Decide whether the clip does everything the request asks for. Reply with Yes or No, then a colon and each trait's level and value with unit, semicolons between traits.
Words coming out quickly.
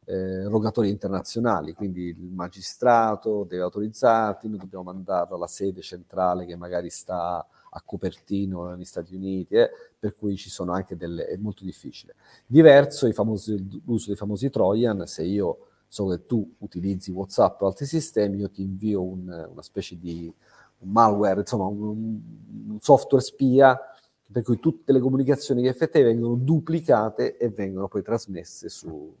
No: average, 155 wpm